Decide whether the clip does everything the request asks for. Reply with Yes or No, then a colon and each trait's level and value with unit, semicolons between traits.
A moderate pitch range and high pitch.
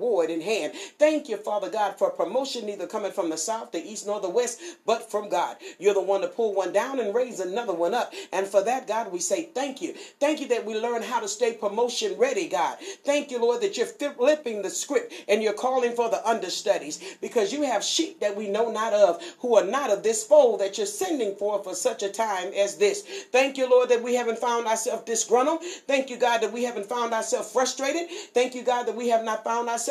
No: wide, 6.1 semitones; high, 240 Hz